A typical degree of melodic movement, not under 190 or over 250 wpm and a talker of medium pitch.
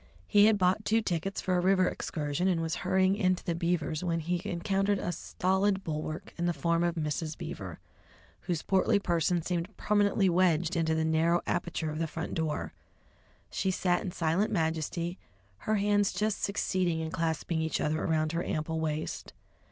No: average, 3.0 semitones; average, 175 wpm; medium, 175 Hz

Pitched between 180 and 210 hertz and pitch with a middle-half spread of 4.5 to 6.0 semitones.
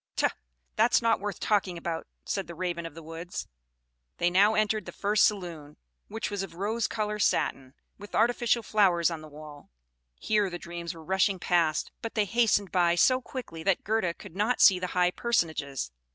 No: medium, 185 Hz; average, 3.9 semitones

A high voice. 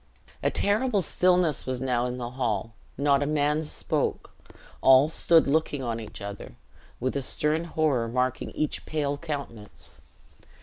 No: medium, 140 Hz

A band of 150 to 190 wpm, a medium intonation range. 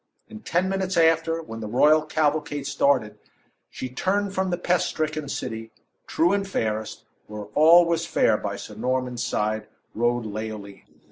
No: average, 155 wpm; wide, 7.2 semitones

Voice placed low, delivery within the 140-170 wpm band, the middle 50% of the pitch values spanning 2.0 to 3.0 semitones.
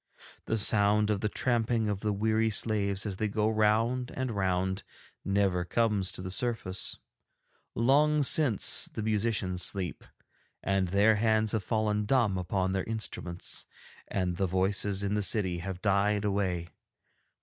Yes: low, 105 Hz; average, 150 wpm; narrow, 2.6 semitones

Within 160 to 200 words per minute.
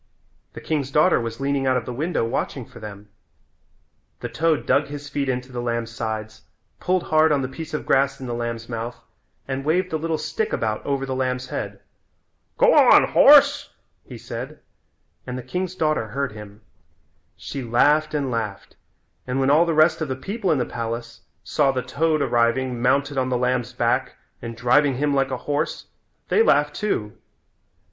Yes: average, 185 wpm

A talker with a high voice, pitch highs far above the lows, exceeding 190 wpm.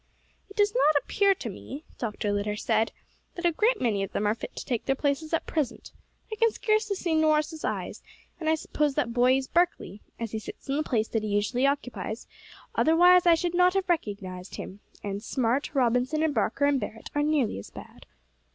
Yes: very high, 275 Hz; wide, 6.7 semitones; fast, 205 wpm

